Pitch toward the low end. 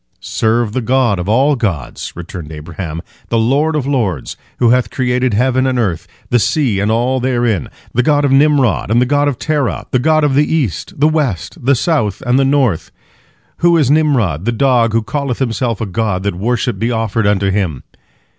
Yes: low, 120 Hz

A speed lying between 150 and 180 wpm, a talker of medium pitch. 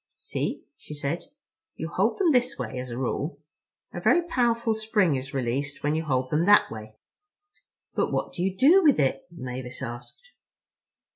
Yes: average, 170 wpm; medium, 150 Hz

